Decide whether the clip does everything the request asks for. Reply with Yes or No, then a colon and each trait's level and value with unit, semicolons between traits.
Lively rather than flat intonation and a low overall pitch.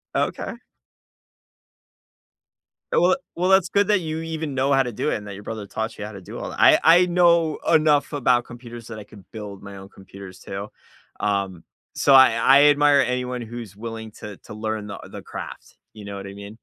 Yes: wide, 6.2 semitones; low, 115 Hz